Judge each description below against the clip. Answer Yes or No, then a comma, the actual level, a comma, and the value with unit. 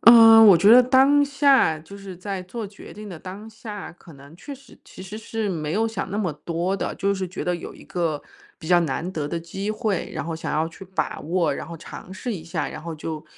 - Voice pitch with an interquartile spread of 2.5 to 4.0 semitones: No, average, 4.5 semitones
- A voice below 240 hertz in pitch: Yes, high, 190 Hz